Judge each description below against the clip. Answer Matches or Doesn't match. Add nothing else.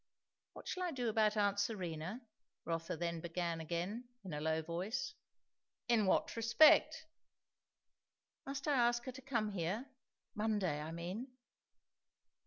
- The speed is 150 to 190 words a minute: Doesn't match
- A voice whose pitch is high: Matches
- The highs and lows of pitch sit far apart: Matches